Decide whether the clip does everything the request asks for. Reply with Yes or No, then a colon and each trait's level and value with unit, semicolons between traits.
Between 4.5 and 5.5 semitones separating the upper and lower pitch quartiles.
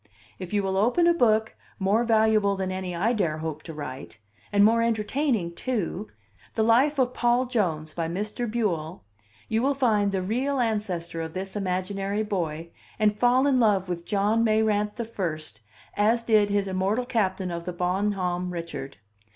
No: average, 4.1 semitones